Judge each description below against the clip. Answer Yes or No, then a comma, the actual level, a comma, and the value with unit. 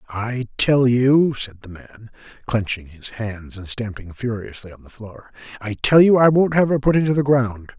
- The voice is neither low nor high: No, low, 120 Hz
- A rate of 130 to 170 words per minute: No, average, 195 wpm